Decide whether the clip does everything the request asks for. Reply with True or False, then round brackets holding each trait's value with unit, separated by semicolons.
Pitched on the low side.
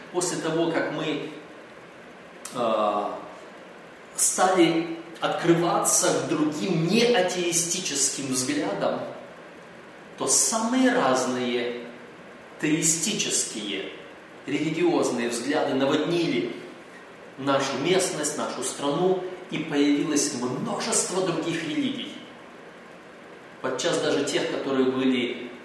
False (165 Hz)